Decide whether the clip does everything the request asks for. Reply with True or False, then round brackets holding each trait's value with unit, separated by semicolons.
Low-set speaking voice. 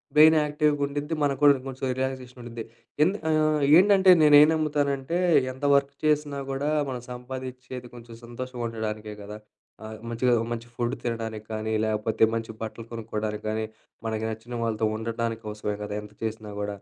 True (120 Hz)